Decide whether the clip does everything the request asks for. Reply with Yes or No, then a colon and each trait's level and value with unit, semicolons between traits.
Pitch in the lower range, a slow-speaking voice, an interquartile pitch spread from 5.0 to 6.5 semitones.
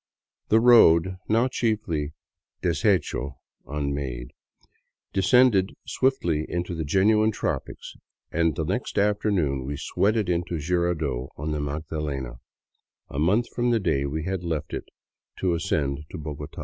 Yes: very low, 85 Hz; slow, 130 wpm; wide, 5.6 semitones